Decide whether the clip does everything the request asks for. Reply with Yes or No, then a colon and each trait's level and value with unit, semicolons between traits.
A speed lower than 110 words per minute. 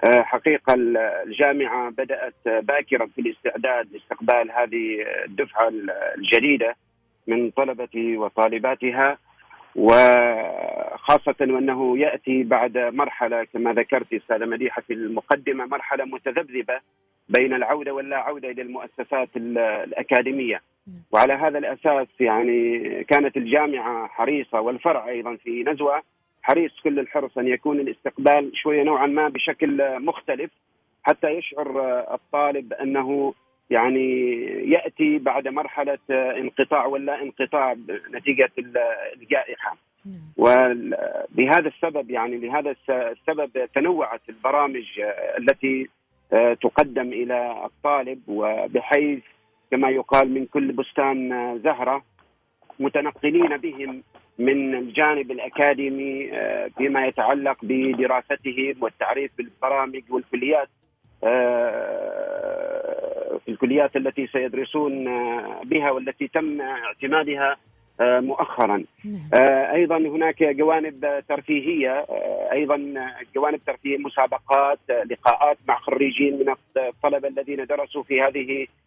Yes: average, 95 wpm